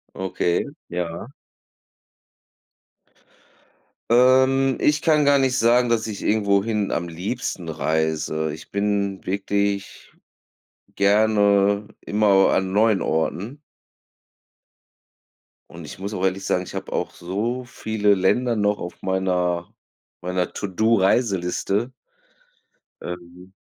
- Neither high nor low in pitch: No, low, 100 Hz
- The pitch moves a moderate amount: Yes, average, 3.4 semitones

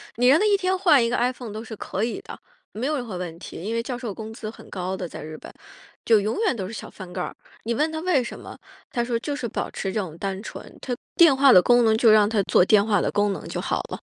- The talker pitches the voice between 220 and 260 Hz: Yes, high, 225 Hz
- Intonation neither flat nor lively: Yes, average, 4.1 semitones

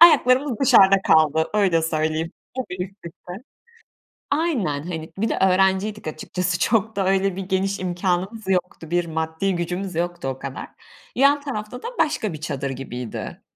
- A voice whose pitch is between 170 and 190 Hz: Yes, medium, 185 Hz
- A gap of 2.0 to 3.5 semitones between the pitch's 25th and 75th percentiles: No, average, 4.7 semitones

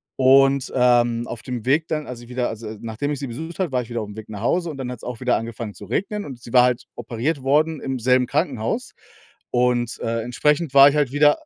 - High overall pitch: No, low, 125 Hz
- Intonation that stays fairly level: No, average, 3.5 semitones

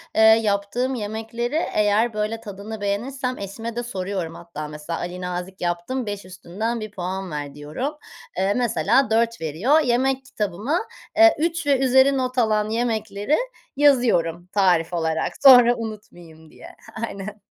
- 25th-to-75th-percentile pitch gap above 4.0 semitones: Yes, average, 5.1 semitones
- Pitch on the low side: No, high, 215 Hz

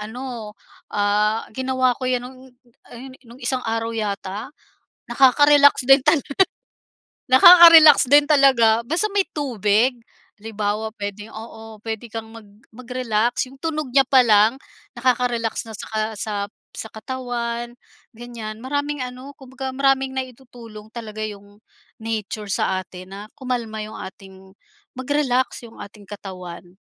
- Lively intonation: No, average, 3.4 semitones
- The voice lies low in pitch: No, high, 235 Hz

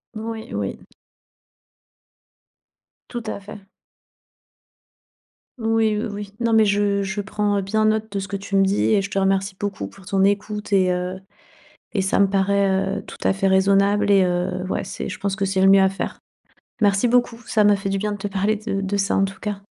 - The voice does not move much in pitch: Yes, narrow, 1.3 semitones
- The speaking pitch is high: Yes, high, 200 Hz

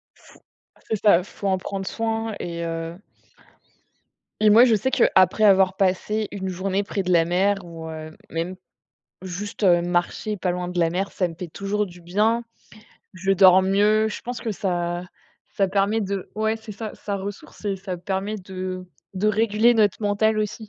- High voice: Yes, high, 195 Hz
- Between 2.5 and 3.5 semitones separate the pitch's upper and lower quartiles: Yes, average, 2.9 semitones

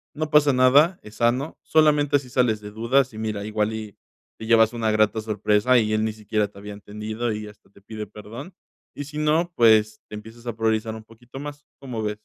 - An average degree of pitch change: Yes, average, 3.4 semitones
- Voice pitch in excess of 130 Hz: No, low, 110 Hz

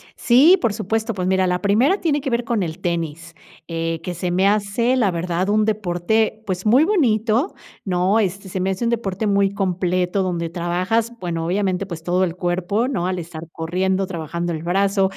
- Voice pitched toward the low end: No, high, 190 Hz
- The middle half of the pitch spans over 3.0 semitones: Yes, average, 3.7 semitones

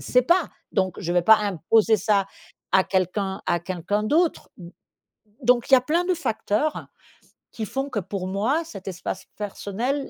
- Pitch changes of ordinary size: No, wide, 5.7 semitones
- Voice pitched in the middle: No, high, 210 Hz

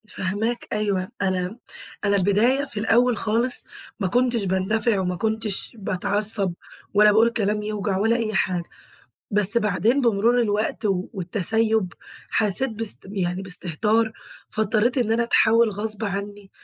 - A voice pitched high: Yes, high, 210 Hz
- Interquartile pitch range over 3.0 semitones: No, average, 2.7 semitones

